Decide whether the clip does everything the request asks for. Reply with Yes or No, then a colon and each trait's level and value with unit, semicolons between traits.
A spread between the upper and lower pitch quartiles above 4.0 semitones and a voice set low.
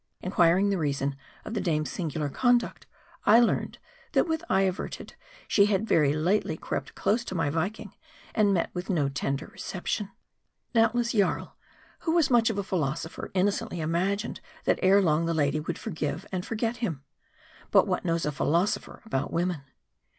No: average, 5.1 semitones; medium, 185 Hz